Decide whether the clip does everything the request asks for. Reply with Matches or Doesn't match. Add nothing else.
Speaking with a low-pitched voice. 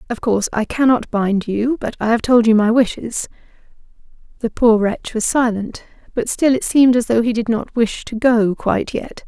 Doesn't match